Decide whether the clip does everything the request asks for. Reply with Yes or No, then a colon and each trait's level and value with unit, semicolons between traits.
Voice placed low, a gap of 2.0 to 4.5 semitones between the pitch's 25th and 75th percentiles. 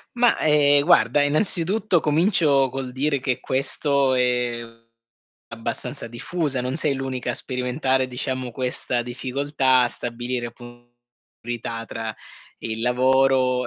Yes: low, 130 Hz; narrow, 2.6 semitones